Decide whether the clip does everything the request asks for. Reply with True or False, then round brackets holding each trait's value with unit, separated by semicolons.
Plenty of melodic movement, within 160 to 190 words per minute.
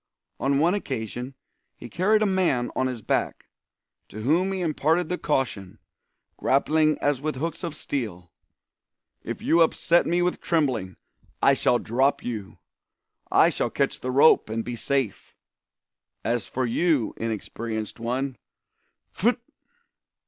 False (6.0 semitones; 135 wpm)